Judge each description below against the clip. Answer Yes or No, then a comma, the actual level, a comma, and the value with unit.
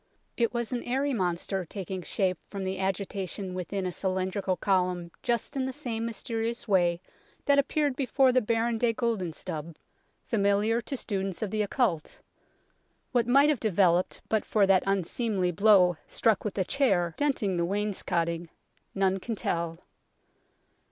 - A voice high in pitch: Yes, high, 200 Hz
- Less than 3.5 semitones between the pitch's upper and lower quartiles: No, average, 4.2 semitones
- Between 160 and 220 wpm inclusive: No, average, 150 wpm